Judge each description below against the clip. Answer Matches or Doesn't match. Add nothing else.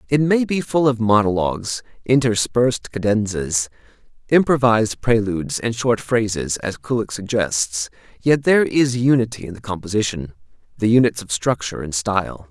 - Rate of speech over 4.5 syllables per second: Matches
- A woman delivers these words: Doesn't match